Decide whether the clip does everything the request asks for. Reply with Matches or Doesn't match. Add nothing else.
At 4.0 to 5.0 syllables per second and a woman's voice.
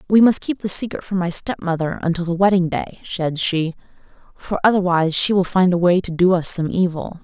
Doesn't match